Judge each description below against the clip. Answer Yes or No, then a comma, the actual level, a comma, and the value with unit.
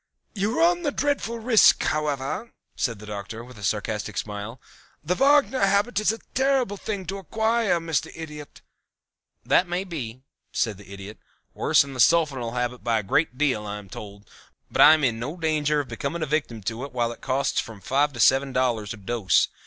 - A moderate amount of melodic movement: No, wide, 8.6 semitones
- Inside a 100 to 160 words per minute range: No, average, 195 wpm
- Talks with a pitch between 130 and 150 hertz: Yes, medium, 140 Hz